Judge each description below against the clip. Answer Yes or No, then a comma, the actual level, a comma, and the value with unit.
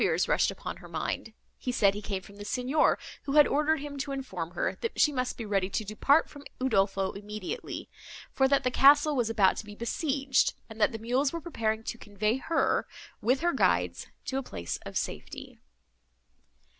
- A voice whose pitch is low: No, very high, 250 Hz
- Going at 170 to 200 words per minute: Yes, average, 195 wpm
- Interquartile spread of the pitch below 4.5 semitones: No, average, 5.2 semitones